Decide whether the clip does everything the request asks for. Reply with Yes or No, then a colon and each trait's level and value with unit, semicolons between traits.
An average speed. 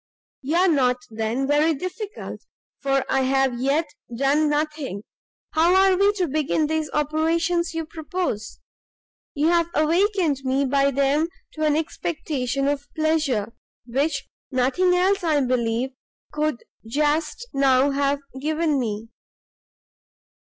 No: slow, 125 wpm